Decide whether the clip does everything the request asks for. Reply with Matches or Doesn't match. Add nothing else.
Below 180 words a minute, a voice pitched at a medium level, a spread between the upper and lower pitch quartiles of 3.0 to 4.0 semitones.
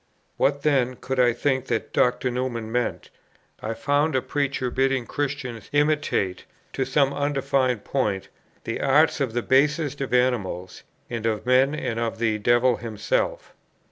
Doesn't match